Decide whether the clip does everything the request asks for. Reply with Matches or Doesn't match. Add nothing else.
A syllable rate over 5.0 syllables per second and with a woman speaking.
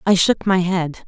Doesn't match